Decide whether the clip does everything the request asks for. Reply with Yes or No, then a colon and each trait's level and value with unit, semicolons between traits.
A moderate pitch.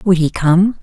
Yes: medium, 180 Hz